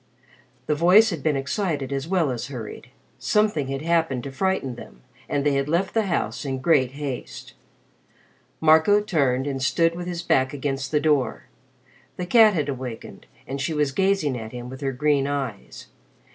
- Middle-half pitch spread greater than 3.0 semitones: Yes, average, 4.1 semitones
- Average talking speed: Yes, average, 175 wpm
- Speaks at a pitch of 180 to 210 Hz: No, medium, 145 Hz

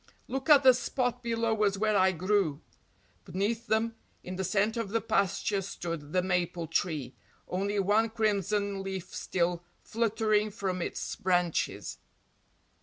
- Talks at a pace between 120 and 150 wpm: Yes, average, 140 wpm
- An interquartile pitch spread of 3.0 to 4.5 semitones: Yes, average, 3.4 semitones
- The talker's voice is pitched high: Yes, high, 200 Hz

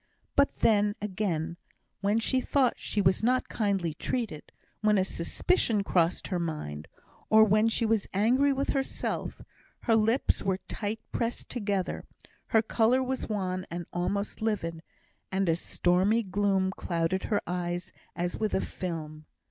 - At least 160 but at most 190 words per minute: No, average, 150 wpm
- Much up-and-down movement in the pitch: No, average, 4.0 semitones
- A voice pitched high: Yes, high, 200 Hz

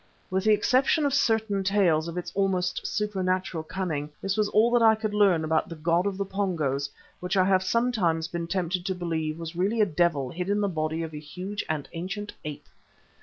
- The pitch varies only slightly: No, average, 4.0 semitones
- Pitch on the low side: No, medium, 185 Hz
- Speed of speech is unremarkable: No, fast, 210 wpm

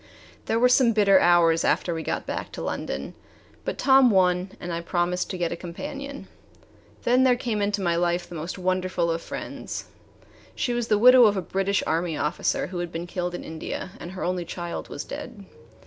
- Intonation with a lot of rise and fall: No, average, 3.9 semitones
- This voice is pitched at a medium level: Yes, medium, 180 Hz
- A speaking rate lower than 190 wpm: No, average, 200 wpm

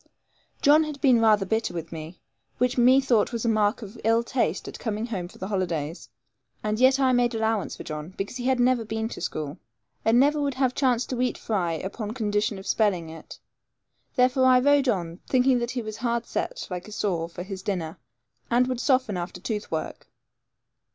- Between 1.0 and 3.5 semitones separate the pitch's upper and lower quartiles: No, average, 4.8 semitones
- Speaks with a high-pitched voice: Yes, high, 225 Hz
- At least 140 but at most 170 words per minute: No, average, 200 wpm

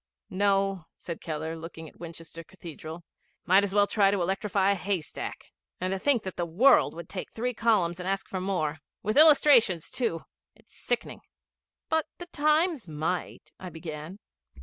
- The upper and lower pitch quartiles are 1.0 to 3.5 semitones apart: No, average, 4.0 semitones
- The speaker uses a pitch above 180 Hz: Yes, high, 190 Hz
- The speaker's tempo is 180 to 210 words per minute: No, average, 165 wpm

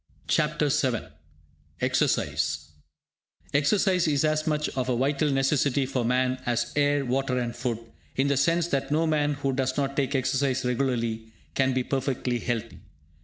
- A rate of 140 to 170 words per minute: Yes, average, 155 wpm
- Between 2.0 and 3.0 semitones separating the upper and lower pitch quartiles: Yes, narrow, 2.4 semitones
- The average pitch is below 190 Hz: Yes, low, 135 Hz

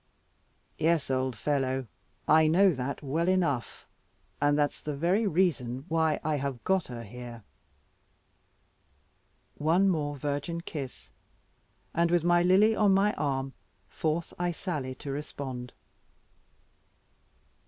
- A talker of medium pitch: Yes, medium, 150 Hz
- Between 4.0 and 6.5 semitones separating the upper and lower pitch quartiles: Yes, average, 4.5 semitones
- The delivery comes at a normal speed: No, slow, 115 wpm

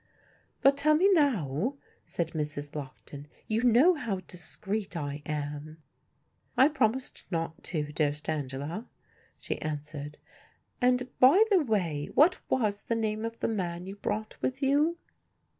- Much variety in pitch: Yes, wide, 9.0 semitones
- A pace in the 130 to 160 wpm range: Yes, average, 140 wpm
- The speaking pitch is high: Yes, high, 200 Hz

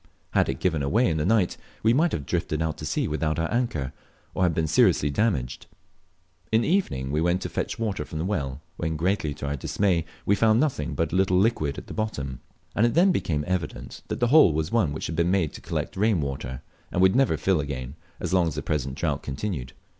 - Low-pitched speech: Yes, very low, 80 Hz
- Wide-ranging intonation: Yes, wide, 5.9 semitones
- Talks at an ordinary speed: No, fast, 235 wpm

